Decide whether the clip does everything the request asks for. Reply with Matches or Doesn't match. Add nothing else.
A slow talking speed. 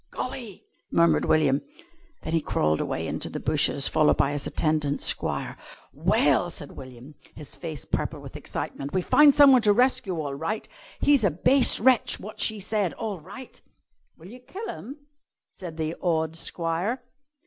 Doesn't match